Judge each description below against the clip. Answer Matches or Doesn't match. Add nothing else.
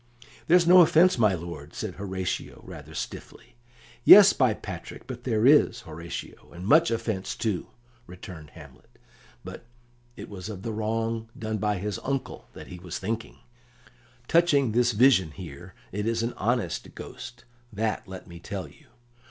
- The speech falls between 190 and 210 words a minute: Doesn't match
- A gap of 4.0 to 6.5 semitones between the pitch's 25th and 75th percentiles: Matches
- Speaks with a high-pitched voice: Doesn't match